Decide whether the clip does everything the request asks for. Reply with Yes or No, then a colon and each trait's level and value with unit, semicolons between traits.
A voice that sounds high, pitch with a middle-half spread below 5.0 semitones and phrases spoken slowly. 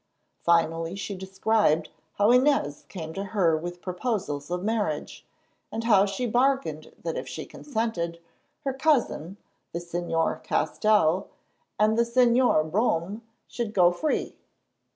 No: high, 195 Hz; wide, 5.4 semitones; slow, 130 wpm